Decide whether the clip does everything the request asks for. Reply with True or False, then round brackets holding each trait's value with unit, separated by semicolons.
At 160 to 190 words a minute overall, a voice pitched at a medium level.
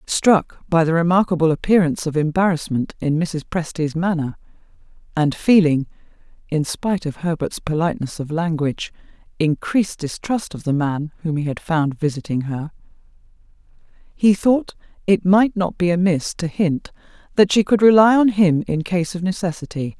False (145 wpm; 170 Hz)